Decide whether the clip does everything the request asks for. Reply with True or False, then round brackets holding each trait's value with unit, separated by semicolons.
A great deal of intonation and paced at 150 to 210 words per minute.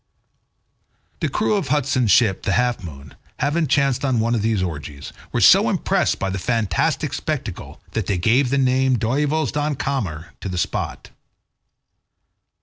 True (6.2 semitones; 155 wpm)